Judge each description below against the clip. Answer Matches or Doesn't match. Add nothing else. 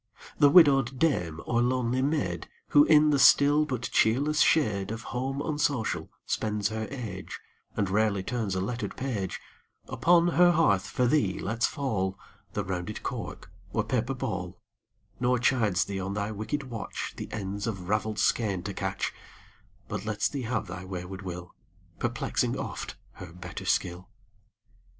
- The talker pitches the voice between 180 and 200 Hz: Doesn't match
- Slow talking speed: Doesn't match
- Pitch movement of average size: Doesn't match